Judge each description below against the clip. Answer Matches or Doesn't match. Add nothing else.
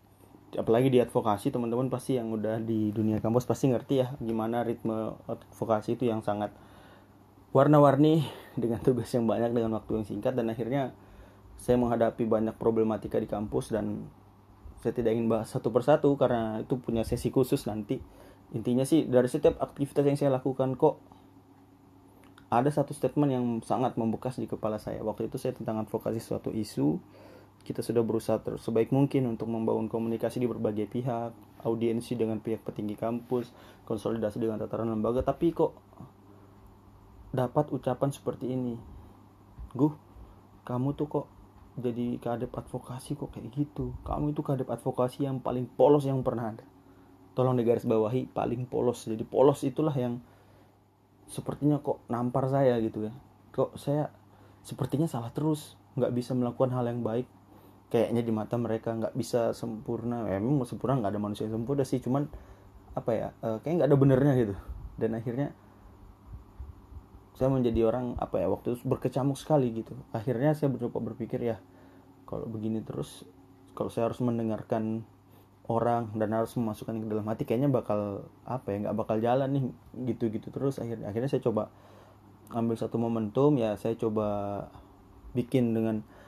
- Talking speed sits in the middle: Doesn't match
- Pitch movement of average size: Matches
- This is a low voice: Matches